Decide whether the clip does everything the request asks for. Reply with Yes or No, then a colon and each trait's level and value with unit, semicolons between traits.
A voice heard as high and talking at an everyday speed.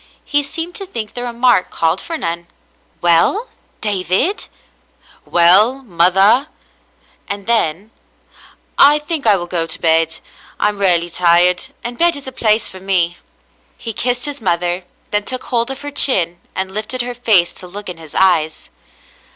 Yes: high, 200 Hz; average, 170 wpm